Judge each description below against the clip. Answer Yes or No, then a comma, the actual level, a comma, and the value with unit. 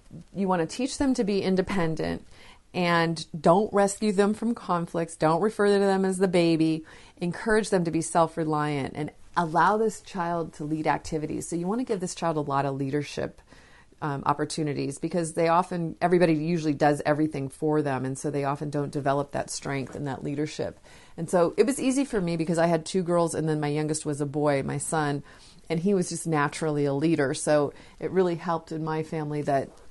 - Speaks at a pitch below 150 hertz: No, medium, 165 Hz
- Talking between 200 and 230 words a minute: Yes, fast, 205 wpm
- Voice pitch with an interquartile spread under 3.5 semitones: Yes, average, 3.1 semitones